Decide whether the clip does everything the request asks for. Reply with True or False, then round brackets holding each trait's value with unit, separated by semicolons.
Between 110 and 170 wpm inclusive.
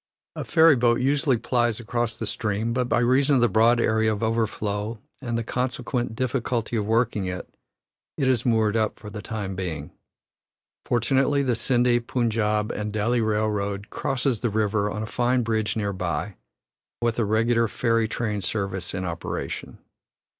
True (160 wpm)